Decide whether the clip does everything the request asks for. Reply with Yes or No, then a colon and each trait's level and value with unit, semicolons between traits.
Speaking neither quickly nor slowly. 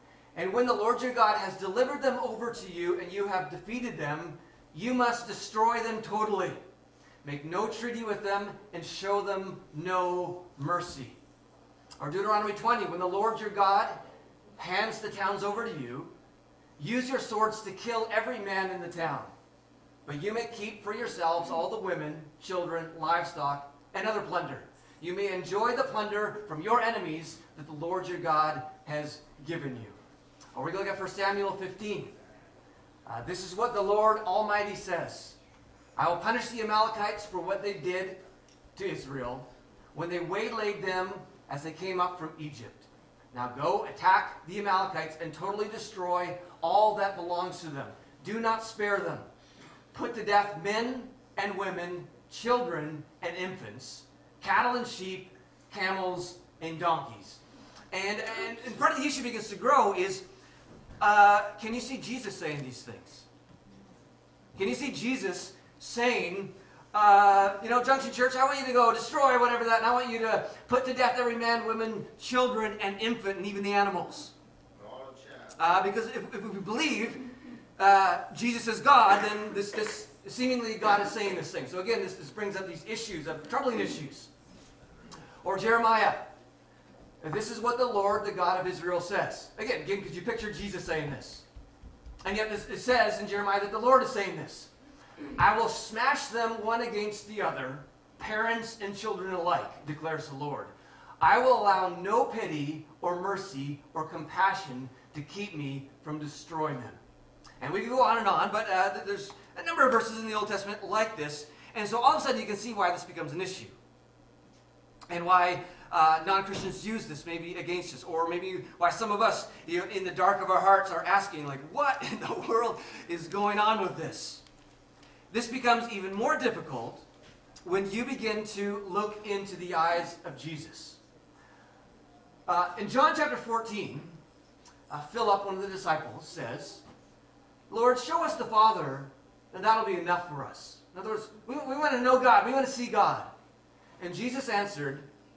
Yes: average, 175 wpm